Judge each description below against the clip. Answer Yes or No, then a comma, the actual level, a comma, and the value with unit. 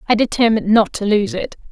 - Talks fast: Yes, fast, 210 wpm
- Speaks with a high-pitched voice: Yes, high, 210 Hz